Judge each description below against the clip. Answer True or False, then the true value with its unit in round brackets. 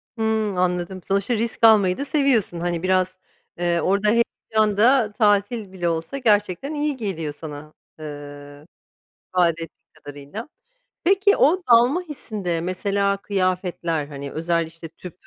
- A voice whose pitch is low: False (190 Hz)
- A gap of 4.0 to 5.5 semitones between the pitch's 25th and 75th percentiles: True (4.8 semitones)